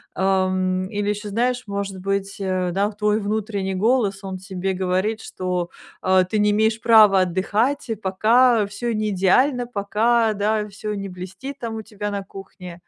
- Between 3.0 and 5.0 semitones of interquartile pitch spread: No, narrow, 2.5 semitones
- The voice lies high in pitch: Yes, high, 200 Hz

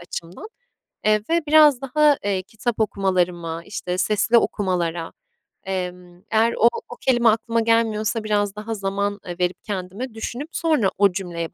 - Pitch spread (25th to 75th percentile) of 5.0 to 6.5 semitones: No, average, 4.1 semitones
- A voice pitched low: No, high, 205 Hz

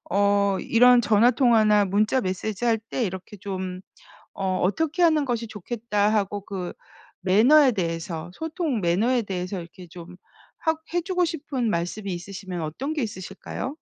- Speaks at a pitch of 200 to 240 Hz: Yes, high, 210 Hz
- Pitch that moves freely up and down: No, average, 4.9 semitones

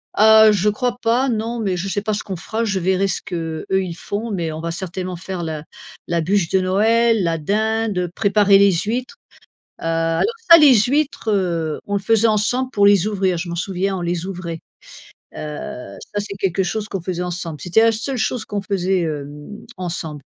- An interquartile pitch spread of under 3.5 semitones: No, average, 3.9 semitones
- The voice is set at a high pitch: Yes, high, 195 Hz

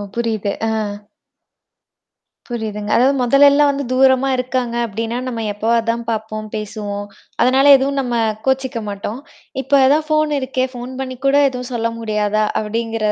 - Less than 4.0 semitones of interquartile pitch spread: Yes, average, 3.4 semitones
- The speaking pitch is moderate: No, high, 240 Hz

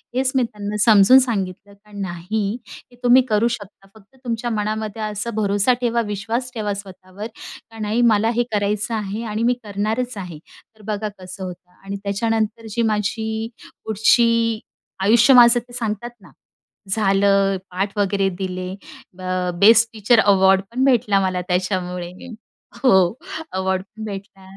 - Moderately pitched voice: No, high, 210 Hz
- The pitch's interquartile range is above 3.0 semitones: No, average, 2.7 semitones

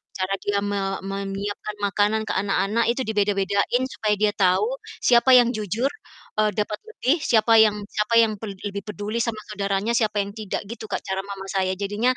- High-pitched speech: Yes, high, 210 Hz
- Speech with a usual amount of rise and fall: No, narrow, 2.1 semitones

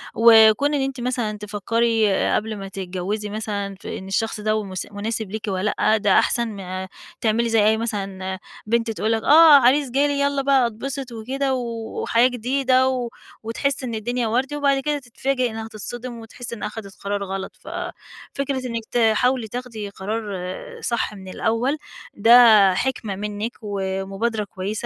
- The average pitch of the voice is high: Yes, high, 225 Hz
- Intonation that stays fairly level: No, average, 3.3 semitones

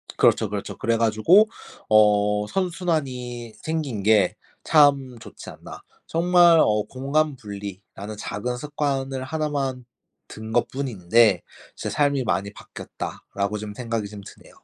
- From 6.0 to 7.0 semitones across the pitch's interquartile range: No, wide, 5.5 semitones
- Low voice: Yes, low, 120 Hz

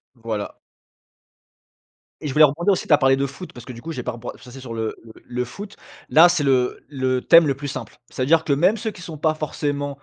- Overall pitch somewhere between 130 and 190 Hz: Yes, medium, 140 Hz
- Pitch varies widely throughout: No, average, 4.1 semitones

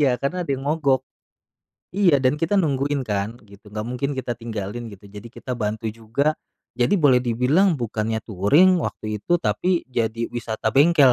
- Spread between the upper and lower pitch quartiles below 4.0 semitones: No, average, 4.4 semitones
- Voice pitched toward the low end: Yes, low, 125 Hz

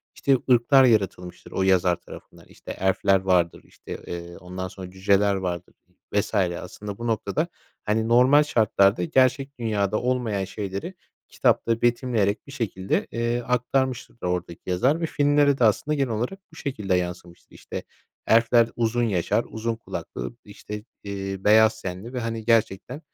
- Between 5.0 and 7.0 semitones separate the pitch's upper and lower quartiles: No, average, 4.4 semitones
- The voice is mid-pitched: No, low, 110 Hz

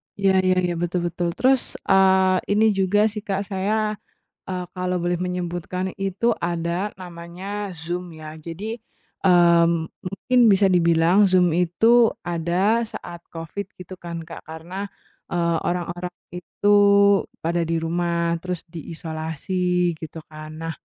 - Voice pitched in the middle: Yes, medium, 180 Hz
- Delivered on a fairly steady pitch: Yes, narrow, 2.2 semitones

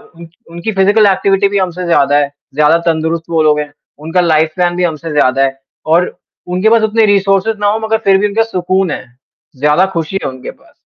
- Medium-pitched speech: Yes, medium, 175 Hz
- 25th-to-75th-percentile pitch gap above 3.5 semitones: Yes, average, 4.1 semitones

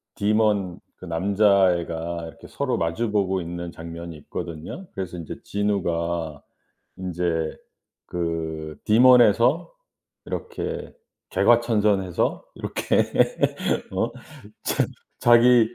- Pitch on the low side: Yes, very low, 90 Hz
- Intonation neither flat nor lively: Yes, average, 4.3 semitones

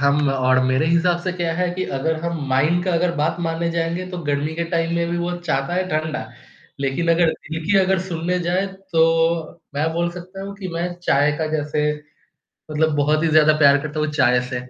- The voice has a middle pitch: Yes, medium, 165 Hz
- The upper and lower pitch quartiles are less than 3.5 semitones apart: Yes, average, 2.7 semitones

